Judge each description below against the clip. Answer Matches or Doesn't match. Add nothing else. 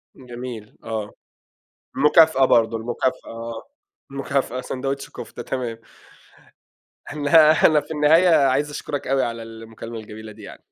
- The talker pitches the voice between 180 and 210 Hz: Doesn't match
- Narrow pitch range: Doesn't match